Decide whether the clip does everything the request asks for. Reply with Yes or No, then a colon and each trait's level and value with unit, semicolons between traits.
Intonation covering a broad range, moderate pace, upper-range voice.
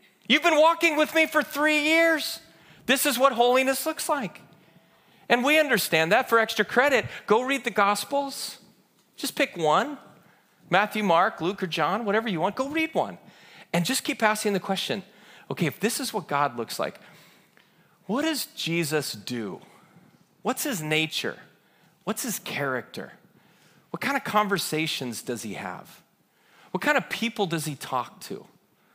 Yes: wide, 8.3 semitones; average, 160 wpm; high, 210 Hz